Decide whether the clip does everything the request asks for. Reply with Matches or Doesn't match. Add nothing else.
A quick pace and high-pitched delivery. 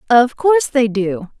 Doesn't match